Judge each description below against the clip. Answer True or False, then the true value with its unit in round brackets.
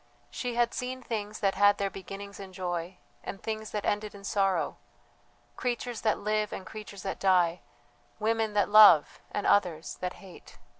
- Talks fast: False (165 wpm)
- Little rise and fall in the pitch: True (2.2 semitones)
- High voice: True (205 Hz)